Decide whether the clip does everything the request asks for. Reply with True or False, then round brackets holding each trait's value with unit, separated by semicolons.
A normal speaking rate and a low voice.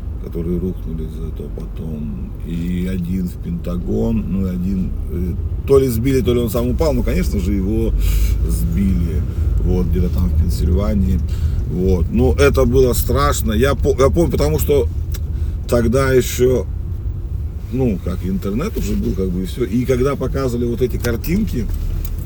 True (150 wpm; 90 Hz)